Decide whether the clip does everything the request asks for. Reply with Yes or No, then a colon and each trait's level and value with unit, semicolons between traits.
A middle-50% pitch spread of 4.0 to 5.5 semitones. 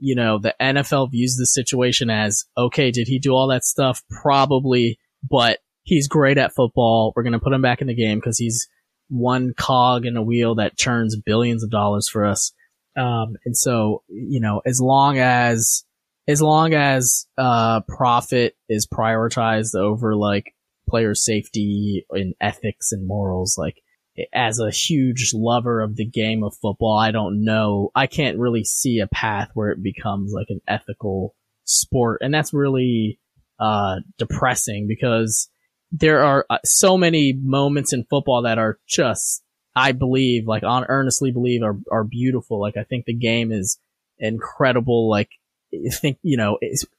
No: average, 3.1 semitones